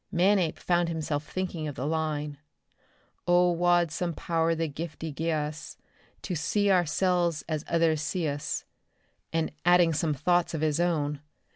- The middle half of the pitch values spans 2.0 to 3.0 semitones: Yes, narrow, 2.6 semitones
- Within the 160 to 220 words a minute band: No, average, 150 wpm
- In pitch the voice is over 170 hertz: No, medium, 165 Hz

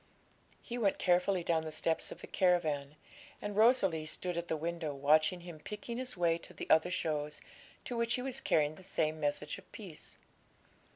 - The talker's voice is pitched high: No, medium, 170 Hz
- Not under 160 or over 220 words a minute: Yes, average, 185 wpm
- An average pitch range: Yes, average, 4.2 semitones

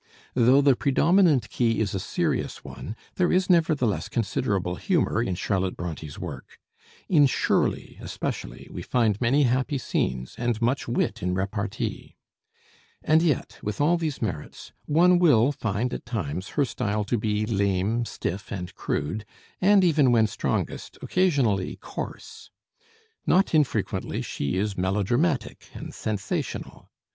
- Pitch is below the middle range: Yes, low, 115 Hz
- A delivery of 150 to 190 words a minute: No, slow, 135 wpm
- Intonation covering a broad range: Yes, wide, 6.5 semitones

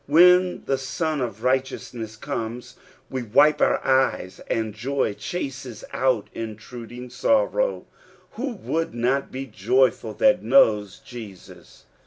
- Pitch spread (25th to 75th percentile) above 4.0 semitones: Yes, average, 4.6 semitones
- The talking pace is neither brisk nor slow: No, slow, 120 wpm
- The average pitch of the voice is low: Yes, low, 125 Hz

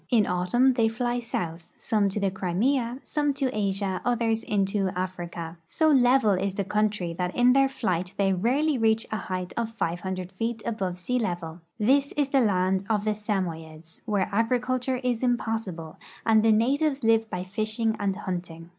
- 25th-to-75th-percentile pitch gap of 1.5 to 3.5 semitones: No, average, 4.6 semitones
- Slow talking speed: No, average, 180 wpm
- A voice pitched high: Yes, high, 215 Hz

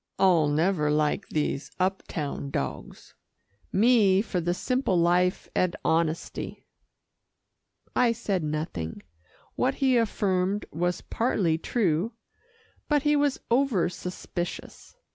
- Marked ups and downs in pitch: Yes, wide, 6.2 semitones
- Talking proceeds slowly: Yes, slow, 110 wpm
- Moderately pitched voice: Yes, medium, 180 Hz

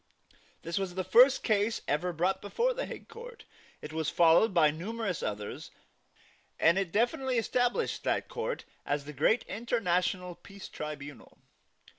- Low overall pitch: No, high, 190 Hz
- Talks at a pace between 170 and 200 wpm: No, average, 145 wpm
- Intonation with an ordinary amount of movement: No, wide, 6.2 semitones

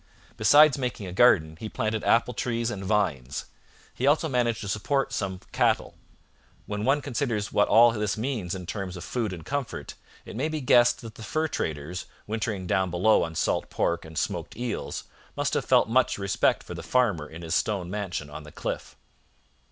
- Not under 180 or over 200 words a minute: Yes, average, 190 wpm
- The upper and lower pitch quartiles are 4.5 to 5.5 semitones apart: Yes, average, 5.2 semitones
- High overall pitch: No, low, 105 Hz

